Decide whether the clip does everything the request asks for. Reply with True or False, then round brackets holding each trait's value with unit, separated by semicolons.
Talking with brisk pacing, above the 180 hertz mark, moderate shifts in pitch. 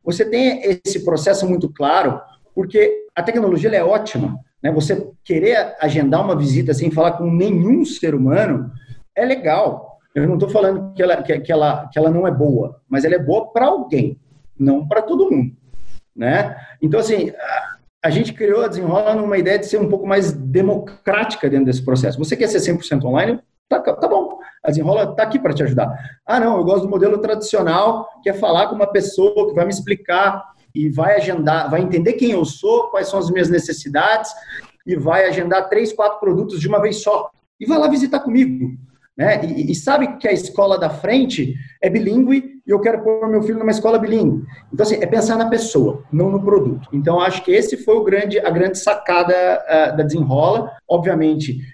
False (200 wpm; 190 Hz; 5.7 semitones)